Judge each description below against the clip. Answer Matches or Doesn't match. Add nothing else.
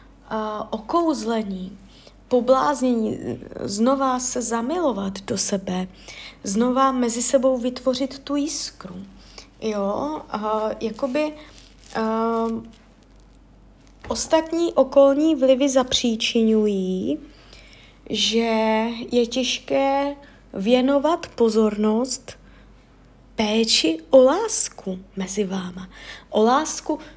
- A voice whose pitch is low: Doesn't match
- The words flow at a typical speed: Doesn't match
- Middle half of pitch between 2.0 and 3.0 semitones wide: Doesn't match